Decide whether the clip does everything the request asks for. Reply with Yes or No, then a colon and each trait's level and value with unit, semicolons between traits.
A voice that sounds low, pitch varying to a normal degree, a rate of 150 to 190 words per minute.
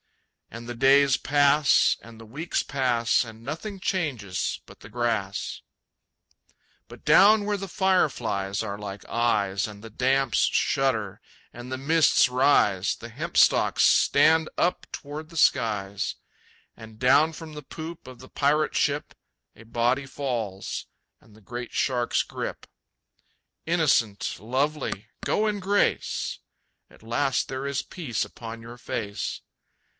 No: low, 130 Hz; average, 5.0 semitones; slow, 135 wpm